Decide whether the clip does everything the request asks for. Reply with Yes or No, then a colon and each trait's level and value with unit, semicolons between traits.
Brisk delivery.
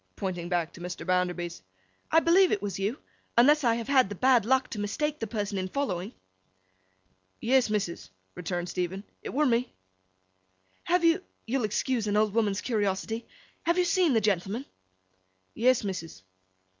No: average, 155 wpm